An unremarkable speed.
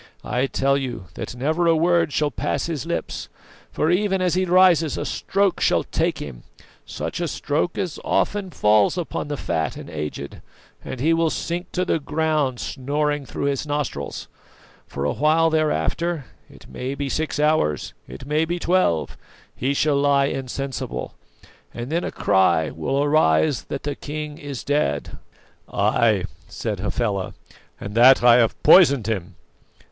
Yes: average, 160 wpm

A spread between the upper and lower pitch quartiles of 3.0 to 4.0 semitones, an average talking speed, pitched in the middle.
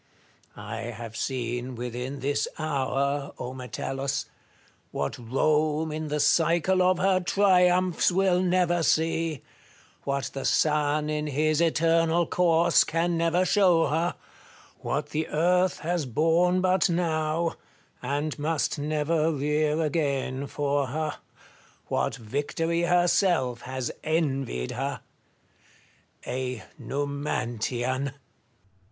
No: average, 3.6 semitones; slow, 110 wpm; medium, 155 Hz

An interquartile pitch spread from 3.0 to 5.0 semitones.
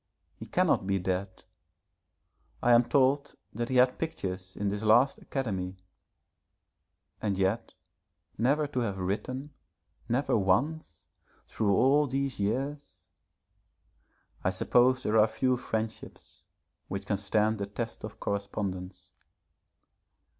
Yes: average, 4.7 semitones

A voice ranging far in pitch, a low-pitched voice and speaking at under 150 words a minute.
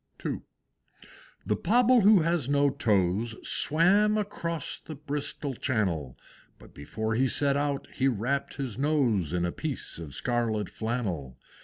Yes: wide, 6.4 semitones; low, 130 Hz; average, 140 wpm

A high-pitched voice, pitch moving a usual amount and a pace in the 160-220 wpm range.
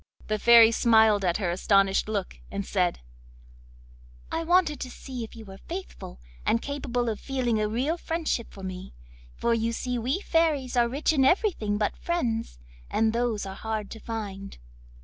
Yes: high, 230 Hz; average, 4.4 semitones; average, 170 wpm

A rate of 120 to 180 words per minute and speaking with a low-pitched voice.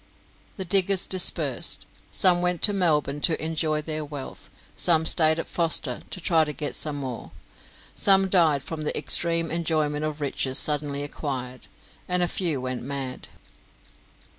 No: average, 145 wpm; medium, 155 Hz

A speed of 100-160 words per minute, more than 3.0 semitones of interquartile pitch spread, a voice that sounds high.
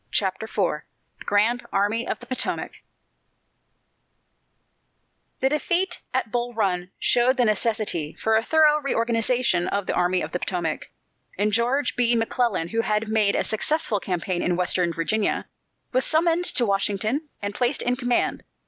Yes: average, 150 wpm; average, 4.1 semitones; high, 220 Hz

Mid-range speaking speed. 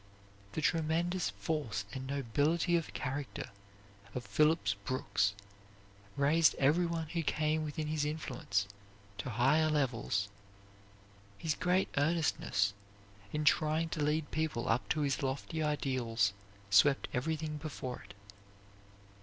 No: slow, 115 wpm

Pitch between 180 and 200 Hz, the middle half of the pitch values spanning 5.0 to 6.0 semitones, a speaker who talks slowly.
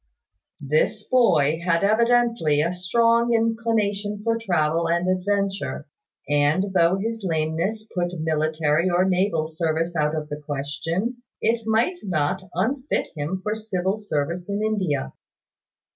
Yes: medium, 185 Hz; wide, 5.5 semitones; slow, 130 wpm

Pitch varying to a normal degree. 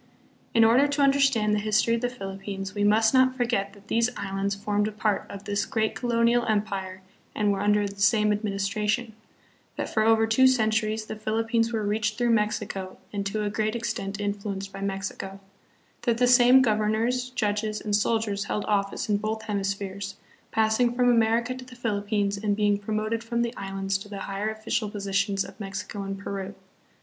No: narrow, 2.3 semitones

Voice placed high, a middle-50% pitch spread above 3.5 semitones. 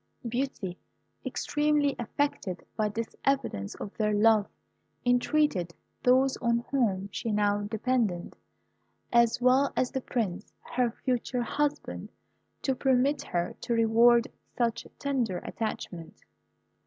Yes: high, 235 Hz; average, 3.9 semitones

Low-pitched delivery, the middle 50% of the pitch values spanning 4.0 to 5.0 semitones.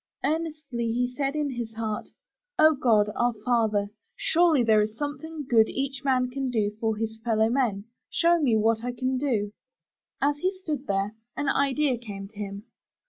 No: high, 245 Hz; average, 4.6 semitones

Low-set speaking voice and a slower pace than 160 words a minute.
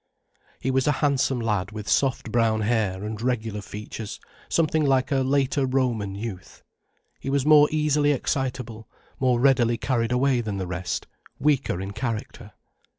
Yes: low, 125 Hz; average, 150 wpm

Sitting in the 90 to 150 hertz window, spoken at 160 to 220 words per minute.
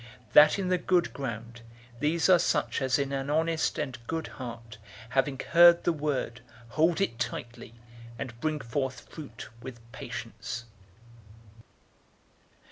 No: medium, 140 Hz; slow, 135 wpm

